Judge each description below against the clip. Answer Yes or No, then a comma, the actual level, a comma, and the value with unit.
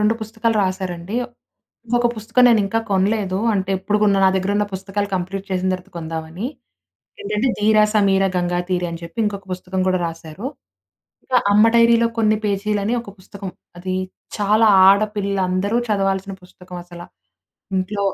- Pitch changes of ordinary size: No, narrow, 2.3 semitones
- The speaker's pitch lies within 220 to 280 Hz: No, high, 195 Hz